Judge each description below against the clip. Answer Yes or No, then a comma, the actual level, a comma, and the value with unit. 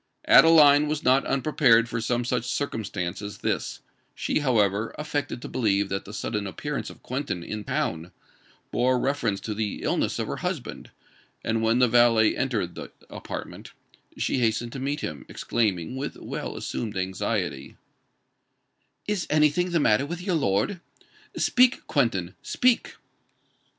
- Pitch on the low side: Yes, low, 120 Hz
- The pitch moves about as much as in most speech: No, wide, 5.7 semitones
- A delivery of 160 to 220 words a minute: No, average, 145 wpm